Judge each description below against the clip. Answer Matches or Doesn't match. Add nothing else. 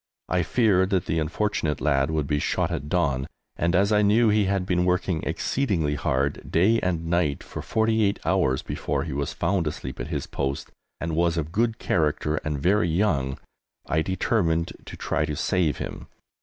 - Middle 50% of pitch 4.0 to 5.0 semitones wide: Matches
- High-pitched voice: Doesn't match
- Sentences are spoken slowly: Doesn't match